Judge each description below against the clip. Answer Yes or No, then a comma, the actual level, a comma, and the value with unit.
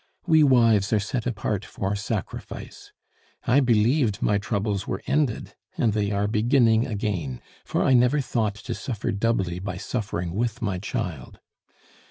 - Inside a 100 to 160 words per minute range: Yes, average, 150 wpm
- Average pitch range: Yes, average, 3.2 semitones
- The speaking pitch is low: Yes, low, 110 Hz